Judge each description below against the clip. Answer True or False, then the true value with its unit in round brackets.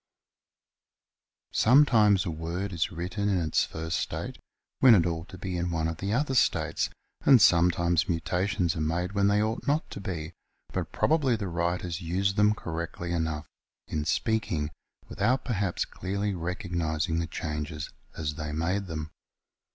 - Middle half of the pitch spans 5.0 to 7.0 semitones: False (3.8 semitones)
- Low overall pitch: True (90 Hz)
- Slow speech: False (155 wpm)